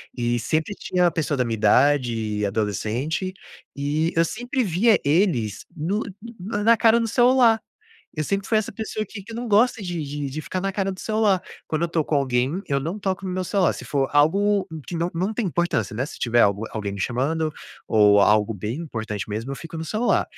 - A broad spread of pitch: Yes, wide, 8.4 semitones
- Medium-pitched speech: Yes, medium, 160 Hz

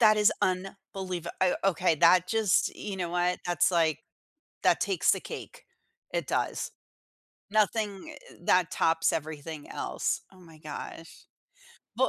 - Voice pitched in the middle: Yes, medium, 180 Hz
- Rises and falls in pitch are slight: No, average, 3.1 semitones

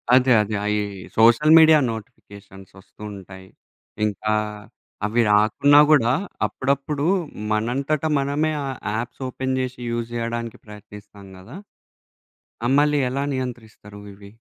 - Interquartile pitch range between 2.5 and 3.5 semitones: No, average, 4.7 semitones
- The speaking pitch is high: No, low, 115 Hz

